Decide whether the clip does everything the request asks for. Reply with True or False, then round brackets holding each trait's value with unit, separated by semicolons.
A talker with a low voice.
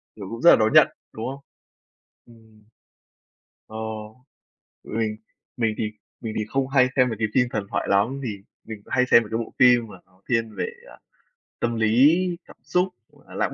True (115 Hz)